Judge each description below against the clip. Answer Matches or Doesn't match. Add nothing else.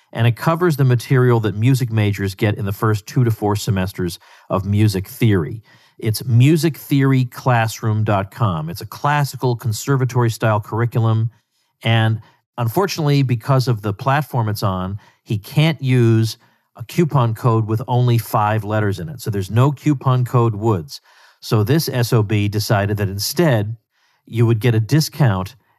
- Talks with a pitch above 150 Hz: Doesn't match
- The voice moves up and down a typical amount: Matches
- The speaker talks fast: Doesn't match